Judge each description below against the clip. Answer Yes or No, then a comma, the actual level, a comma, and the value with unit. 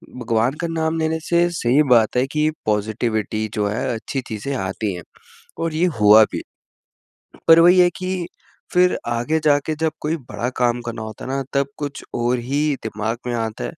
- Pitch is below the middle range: Yes, low, 125 Hz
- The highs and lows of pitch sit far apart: Yes, wide, 6.2 semitones